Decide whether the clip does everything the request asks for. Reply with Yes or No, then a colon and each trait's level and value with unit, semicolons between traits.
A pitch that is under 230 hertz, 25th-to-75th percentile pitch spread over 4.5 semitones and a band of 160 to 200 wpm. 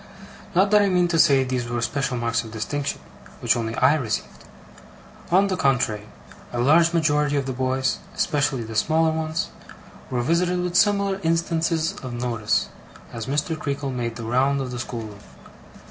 Yes: medium, 140 Hz; wide, 5.4 semitones; average, 170 wpm